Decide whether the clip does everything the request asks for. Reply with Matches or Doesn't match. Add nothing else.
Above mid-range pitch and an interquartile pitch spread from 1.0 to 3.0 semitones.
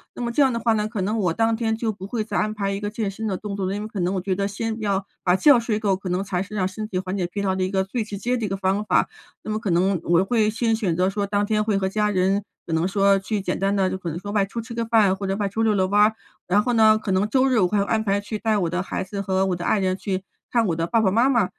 Matches